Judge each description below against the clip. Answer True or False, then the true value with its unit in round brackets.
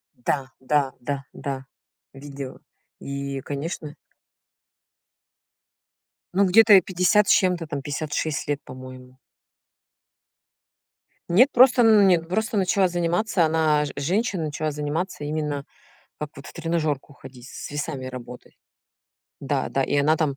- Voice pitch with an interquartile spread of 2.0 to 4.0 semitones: False (4.4 semitones)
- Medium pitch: True (150 Hz)